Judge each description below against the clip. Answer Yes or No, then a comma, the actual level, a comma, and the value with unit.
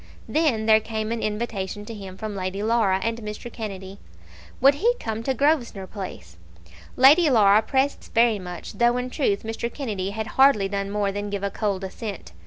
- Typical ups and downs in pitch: Yes, average, 3.2 semitones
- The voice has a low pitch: No, high, 215 Hz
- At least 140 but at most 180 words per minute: No, average, 190 wpm